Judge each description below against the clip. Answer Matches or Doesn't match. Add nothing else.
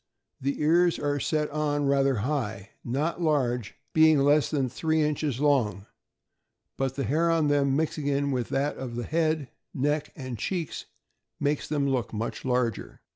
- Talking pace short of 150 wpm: Doesn't match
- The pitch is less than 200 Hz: Matches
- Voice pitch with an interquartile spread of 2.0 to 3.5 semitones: Matches